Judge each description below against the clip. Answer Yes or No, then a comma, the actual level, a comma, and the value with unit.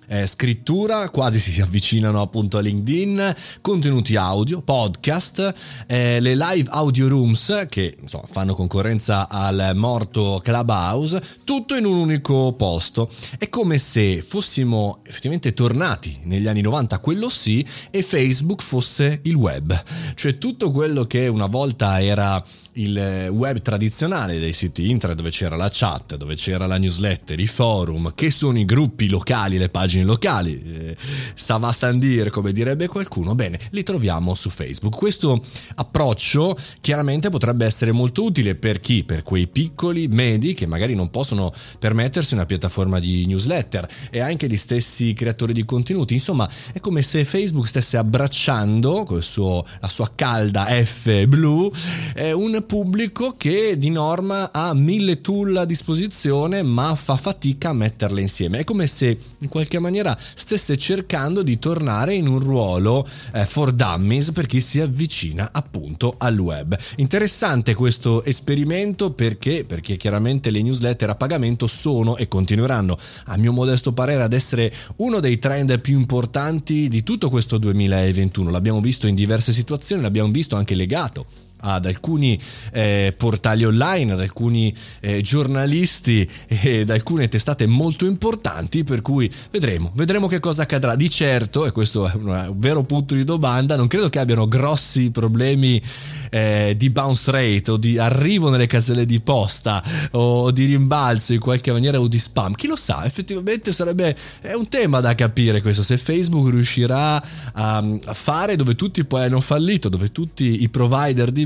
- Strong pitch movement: Yes, wide, 5.8 semitones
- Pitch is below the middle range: Yes, low, 125 Hz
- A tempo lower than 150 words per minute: No, average, 160 wpm